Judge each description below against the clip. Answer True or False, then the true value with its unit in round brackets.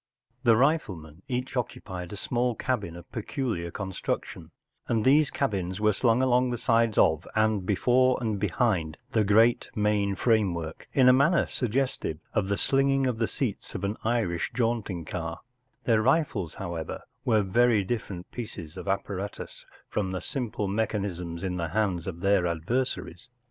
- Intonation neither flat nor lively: True (5.0 semitones)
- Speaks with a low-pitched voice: True (105 Hz)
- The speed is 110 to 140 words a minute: False (160 wpm)